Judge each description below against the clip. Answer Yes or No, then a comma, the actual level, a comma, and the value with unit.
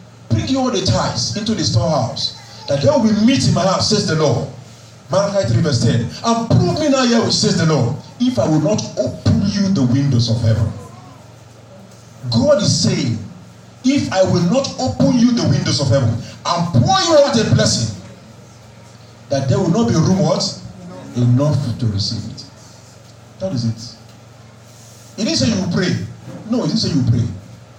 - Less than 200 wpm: No, fast, 205 wpm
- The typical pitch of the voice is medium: No, low, 125 Hz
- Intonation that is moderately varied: No, wide, 7.1 semitones